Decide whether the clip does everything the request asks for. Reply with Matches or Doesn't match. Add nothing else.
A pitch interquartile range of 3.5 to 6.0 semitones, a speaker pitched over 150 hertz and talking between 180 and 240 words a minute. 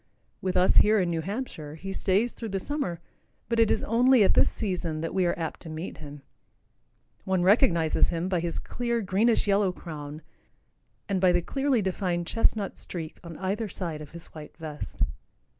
Matches